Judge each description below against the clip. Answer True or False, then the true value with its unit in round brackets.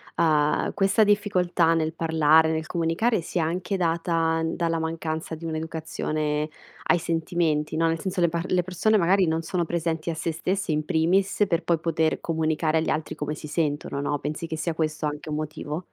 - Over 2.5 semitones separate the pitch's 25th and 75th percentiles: False (1.7 semitones)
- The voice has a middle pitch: True (165 Hz)